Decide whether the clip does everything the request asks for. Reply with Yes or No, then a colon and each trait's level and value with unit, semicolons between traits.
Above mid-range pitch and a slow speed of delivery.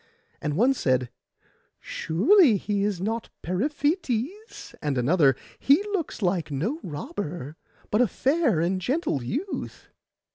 Yes: high, 205 Hz; slow, 120 wpm